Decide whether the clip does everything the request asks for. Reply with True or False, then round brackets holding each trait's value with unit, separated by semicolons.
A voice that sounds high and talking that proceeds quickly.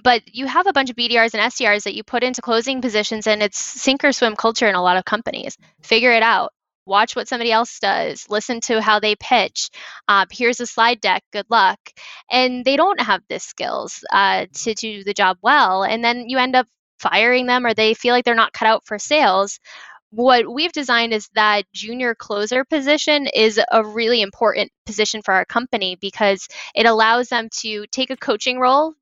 True (230 Hz; 210 wpm)